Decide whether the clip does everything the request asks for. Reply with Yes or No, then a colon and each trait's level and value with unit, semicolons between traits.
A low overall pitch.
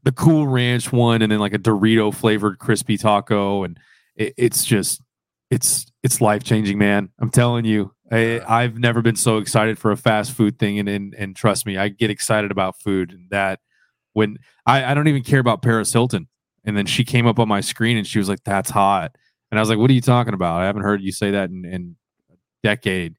Yes: low, 110 Hz